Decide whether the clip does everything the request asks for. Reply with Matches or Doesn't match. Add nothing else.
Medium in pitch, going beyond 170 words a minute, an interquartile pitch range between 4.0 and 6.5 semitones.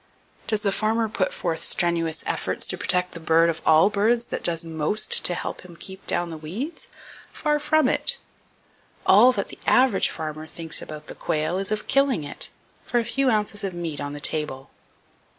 Matches